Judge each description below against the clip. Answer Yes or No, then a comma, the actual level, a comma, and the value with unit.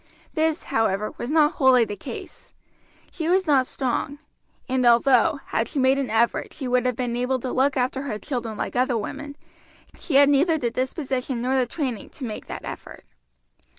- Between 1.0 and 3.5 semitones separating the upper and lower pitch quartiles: Yes, average, 2.9 semitones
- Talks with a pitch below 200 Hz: No, very high, 260 Hz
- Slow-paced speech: No, average, 185 wpm